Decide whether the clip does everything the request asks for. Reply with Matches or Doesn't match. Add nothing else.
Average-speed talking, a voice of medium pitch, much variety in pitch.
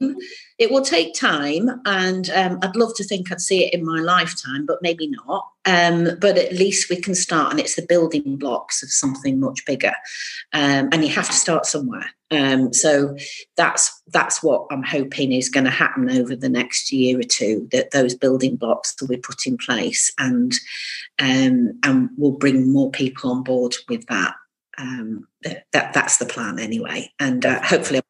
Matches